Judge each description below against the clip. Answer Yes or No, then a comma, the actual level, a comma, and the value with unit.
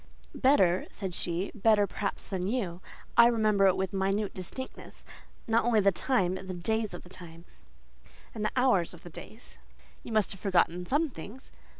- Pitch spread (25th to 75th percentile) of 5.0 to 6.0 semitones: No, average, 3.7 semitones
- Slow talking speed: No, average, 180 wpm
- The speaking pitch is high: Yes, high, 195 Hz